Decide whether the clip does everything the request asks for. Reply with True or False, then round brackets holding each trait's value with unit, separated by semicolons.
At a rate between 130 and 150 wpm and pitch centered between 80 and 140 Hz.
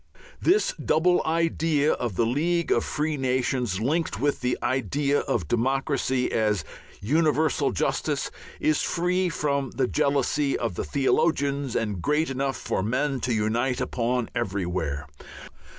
True (135 wpm; 135 Hz)